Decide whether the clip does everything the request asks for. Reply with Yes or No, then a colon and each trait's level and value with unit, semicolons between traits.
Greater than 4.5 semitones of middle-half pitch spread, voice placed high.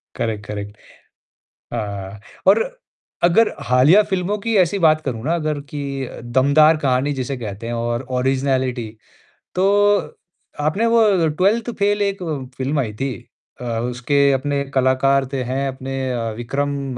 No: average, 5.1 semitones; medium, 140 Hz